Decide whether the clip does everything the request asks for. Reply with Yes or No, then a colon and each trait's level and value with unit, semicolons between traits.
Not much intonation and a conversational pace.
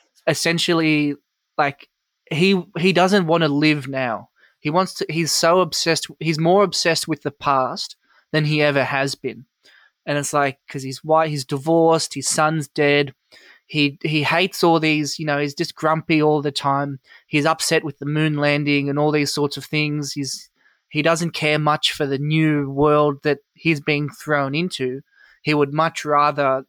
Yes: narrow, 2.2 semitones; average, 180 wpm